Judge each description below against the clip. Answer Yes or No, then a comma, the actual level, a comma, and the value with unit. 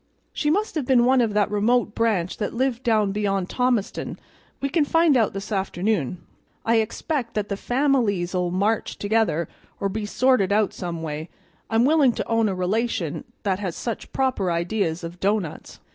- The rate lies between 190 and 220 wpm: No, average, 175 wpm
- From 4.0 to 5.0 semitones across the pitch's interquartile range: Yes, average, 4.6 semitones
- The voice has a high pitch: Yes, high, 210 Hz